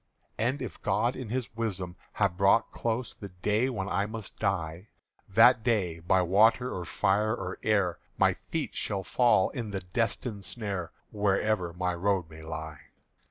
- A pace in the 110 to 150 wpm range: No, average, 160 wpm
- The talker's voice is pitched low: Yes, low, 100 Hz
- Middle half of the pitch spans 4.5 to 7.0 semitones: No, average, 3.7 semitones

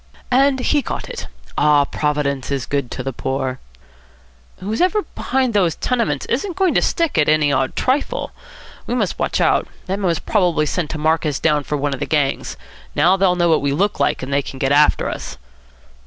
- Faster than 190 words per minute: Yes, average, 200 wpm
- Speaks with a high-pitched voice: No, medium, 160 Hz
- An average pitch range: No, wide, 7.8 semitones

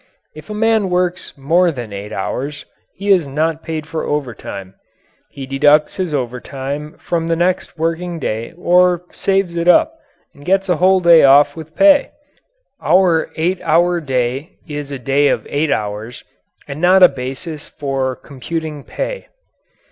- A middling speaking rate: Yes, average, 155 wpm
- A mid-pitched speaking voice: Yes, medium, 155 Hz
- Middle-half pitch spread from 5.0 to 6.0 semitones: No, average, 4.6 semitones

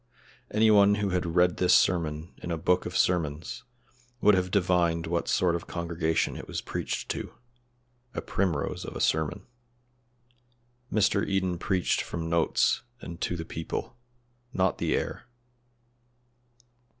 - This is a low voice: Yes, very low, 90 Hz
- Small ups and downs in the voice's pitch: Yes, narrow, 2.1 semitones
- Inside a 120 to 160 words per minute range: Yes, average, 140 wpm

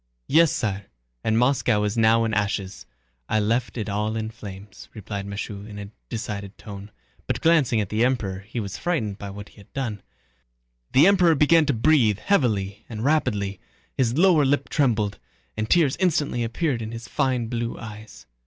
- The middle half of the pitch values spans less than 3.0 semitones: No, average, 4.5 semitones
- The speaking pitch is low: Yes, low, 110 Hz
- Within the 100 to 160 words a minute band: No, average, 175 wpm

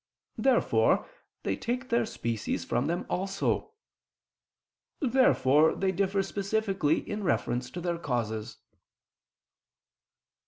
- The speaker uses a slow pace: Yes, slow, 95 wpm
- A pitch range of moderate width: No, wide, 8.4 semitones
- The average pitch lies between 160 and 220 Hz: Yes, high, 190 Hz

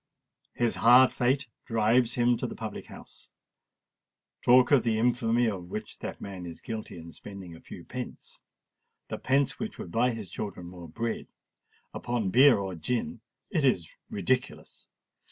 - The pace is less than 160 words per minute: Yes, average, 140 wpm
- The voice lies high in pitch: No, low, 115 Hz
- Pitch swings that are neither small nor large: Yes, average, 4.4 semitones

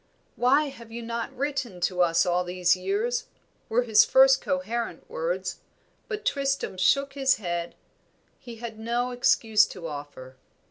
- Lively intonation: Yes, wide, 7.1 semitones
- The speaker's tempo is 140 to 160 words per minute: Yes, average, 145 wpm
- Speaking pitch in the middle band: No, high, 235 Hz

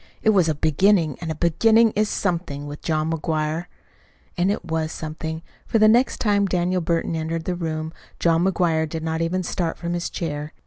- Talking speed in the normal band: Yes, average, 190 wpm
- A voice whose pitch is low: No, medium, 165 Hz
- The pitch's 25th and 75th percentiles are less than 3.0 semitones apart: Yes, narrow, 2.6 semitones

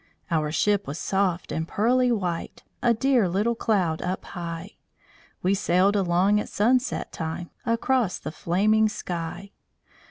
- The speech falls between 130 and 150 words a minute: Yes, slow, 135 wpm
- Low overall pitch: No, high, 195 Hz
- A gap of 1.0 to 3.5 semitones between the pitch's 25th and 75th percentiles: No, average, 4.1 semitones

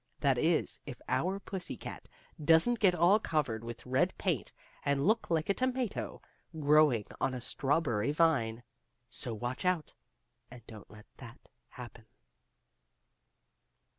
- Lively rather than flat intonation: Yes, wide, 6.4 semitones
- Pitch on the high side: No, medium, 145 Hz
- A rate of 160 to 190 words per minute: No, slow, 135 wpm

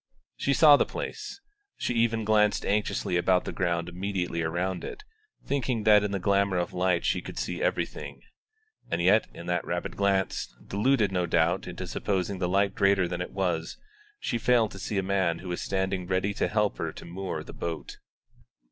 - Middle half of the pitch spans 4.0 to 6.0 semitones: No, average, 2.9 semitones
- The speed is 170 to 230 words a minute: Yes, average, 190 wpm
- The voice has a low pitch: Yes, very low, 95 Hz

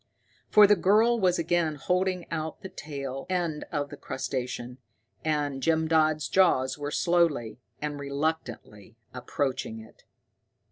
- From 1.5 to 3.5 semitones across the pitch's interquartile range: No, average, 4.5 semitones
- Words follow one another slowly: Yes, slow, 130 wpm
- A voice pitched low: No, medium, 155 Hz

